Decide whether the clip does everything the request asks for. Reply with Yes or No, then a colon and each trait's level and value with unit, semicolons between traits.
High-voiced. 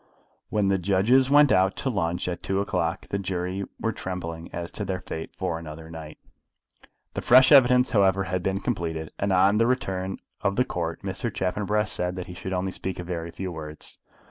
No: very low, 95 Hz